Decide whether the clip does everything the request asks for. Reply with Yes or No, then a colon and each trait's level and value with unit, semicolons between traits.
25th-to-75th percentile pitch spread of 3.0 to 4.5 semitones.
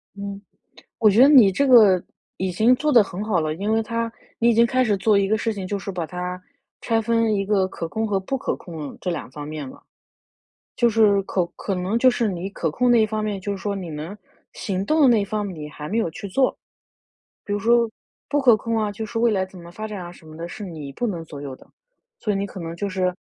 Yes: average, 3.8 semitones